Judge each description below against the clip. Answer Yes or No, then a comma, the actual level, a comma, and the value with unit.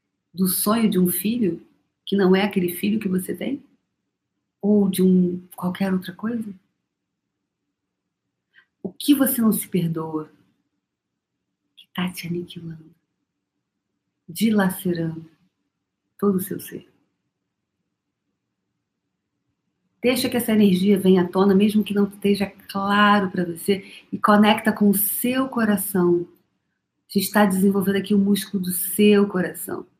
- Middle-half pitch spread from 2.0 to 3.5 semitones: Yes, narrow, 2.5 semitones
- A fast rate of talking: No, average, 125 wpm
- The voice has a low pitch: No, high, 195 Hz